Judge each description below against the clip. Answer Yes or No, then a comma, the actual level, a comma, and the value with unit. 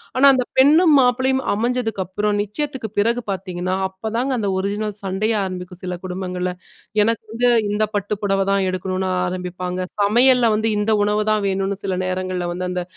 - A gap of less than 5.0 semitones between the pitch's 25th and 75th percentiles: Yes, average, 3.7 semitones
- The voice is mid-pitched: No, high, 200 Hz